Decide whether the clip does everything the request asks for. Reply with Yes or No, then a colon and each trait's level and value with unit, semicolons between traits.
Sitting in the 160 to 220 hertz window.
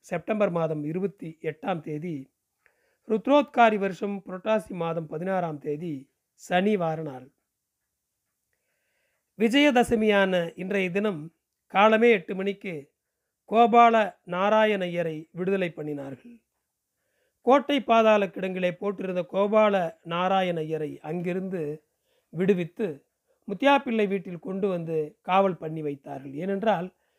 Yes: high, 190 Hz